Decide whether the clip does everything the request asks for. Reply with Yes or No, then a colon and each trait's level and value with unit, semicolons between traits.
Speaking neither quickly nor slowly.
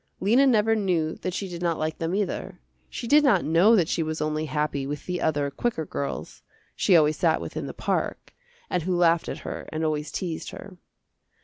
No: fast, 210 wpm